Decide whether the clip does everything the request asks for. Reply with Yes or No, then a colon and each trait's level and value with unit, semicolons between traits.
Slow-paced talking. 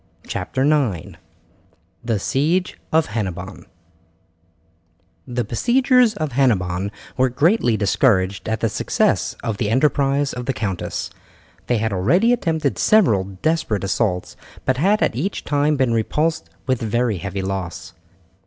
Yes: slow, 125 wpm